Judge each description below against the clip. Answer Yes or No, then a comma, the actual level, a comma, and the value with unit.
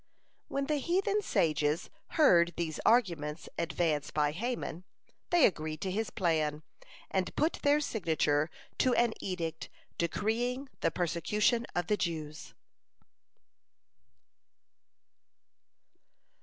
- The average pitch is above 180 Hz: No, medium, 175 Hz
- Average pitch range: No, wide, 7.4 semitones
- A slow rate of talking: Yes, slow, 100 wpm